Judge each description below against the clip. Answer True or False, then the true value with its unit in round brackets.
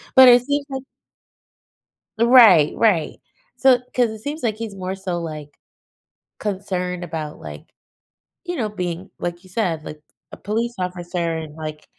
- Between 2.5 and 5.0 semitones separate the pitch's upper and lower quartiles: False (5.6 semitones)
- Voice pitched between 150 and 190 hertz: True (185 Hz)